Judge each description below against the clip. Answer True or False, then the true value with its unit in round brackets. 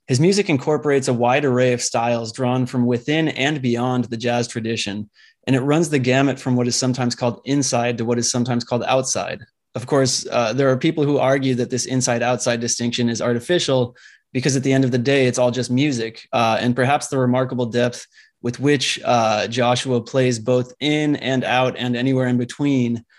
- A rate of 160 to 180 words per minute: False (200 wpm)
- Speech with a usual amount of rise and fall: False (1.8 semitones)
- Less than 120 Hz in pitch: False (125 Hz)